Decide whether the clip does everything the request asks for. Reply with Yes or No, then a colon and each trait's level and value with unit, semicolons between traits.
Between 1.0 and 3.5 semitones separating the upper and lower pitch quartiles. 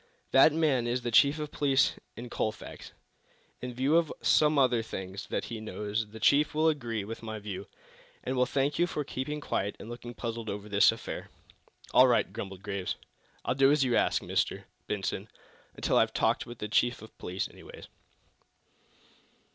No: average, 4.8 semitones